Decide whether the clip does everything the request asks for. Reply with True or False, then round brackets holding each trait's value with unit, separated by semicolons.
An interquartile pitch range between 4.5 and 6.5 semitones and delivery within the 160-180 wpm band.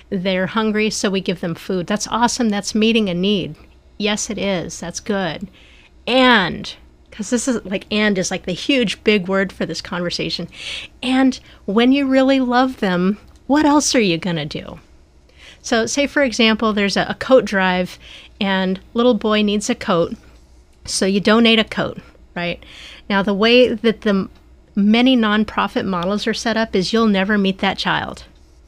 False (3.9 semitones; 175 wpm)